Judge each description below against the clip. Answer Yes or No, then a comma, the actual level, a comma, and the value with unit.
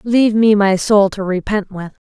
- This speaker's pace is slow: No, fast, 205 wpm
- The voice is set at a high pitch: Yes, high, 205 Hz